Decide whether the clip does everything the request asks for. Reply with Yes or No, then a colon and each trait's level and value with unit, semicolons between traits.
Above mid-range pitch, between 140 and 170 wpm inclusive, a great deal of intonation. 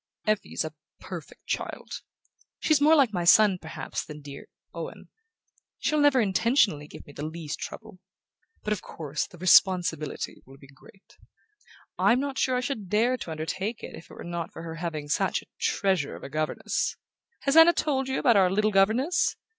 No: high, 195 Hz; average, 180 wpm; wide, 8.1 semitones